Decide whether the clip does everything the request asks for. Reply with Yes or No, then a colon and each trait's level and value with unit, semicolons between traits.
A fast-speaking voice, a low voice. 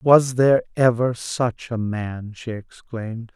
No: average, 145 wpm; low, 120 Hz